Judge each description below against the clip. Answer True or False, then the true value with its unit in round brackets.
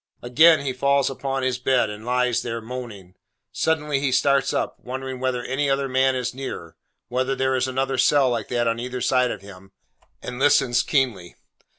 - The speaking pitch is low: True (130 Hz)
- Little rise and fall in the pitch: True (1.9 semitones)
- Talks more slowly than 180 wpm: False (185 wpm)